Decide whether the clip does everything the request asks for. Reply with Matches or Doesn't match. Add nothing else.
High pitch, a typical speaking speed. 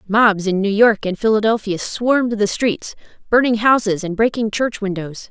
Matches